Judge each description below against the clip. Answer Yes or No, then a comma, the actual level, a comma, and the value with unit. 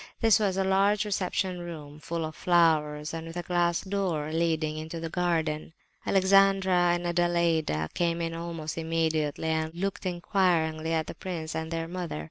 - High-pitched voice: No, medium, 170 Hz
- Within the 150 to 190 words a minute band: Yes, average, 165 wpm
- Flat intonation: Yes, narrow, 2.1 semitones